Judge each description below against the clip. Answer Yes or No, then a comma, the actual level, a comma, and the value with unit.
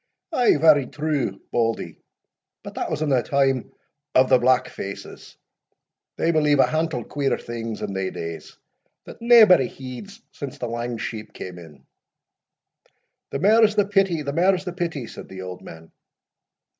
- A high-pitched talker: No, medium, 140 Hz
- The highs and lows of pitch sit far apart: Yes, wide, 6.7 semitones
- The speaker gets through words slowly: No, average, 155 wpm